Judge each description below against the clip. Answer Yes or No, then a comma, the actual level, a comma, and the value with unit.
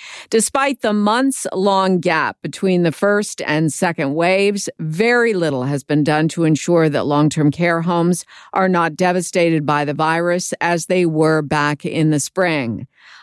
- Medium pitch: Yes, medium, 170 Hz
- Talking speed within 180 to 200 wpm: No, average, 165 wpm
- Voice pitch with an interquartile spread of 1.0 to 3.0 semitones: No, average, 3.6 semitones